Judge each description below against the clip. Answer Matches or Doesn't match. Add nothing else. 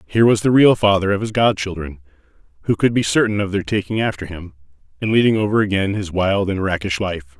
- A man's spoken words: Matches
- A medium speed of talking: Doesn't match